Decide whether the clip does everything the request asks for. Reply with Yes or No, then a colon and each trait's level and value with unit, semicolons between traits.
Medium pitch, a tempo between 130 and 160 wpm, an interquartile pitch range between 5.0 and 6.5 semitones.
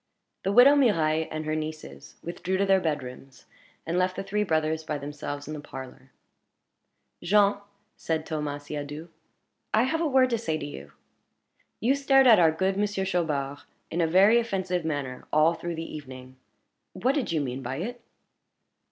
No: medium, 165 Hz; average, 170 wpm; average, 5.3 semitones